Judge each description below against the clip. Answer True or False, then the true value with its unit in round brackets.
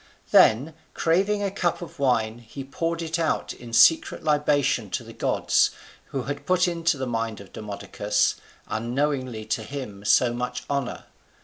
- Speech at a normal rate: True (165 wpm)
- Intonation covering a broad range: True (6.2 semitones)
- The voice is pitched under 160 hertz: True (135 Hz)